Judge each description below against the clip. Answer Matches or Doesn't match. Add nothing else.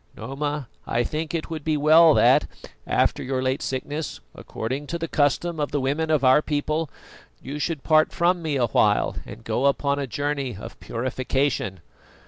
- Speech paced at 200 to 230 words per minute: Doesn't match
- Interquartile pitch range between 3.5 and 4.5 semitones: Doesn't match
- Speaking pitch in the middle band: Matches